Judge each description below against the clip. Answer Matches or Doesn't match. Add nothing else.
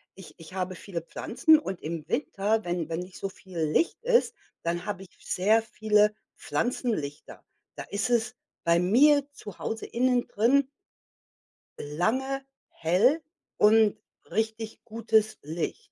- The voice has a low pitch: Doesn't match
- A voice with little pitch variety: Doesn't match